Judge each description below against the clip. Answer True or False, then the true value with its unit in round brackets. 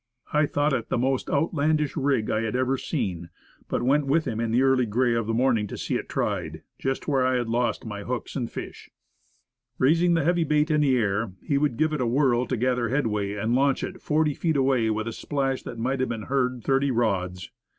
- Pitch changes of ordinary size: True (3.7 semitones)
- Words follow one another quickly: True (225 wpm)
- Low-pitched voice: True (130 Hz)